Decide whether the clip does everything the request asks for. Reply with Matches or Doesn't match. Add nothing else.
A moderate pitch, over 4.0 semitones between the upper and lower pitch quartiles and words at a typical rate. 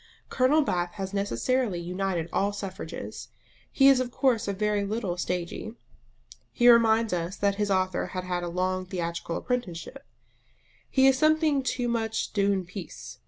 Doesn't match